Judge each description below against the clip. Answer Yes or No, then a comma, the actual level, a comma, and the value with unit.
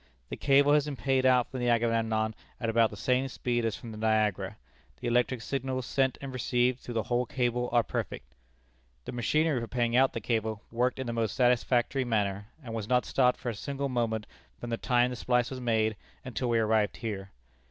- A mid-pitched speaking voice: No, low, 120 Hz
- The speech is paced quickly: Yes, fast, 210 wpm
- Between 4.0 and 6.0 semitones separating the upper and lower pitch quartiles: No, narrow, 2.4 semitones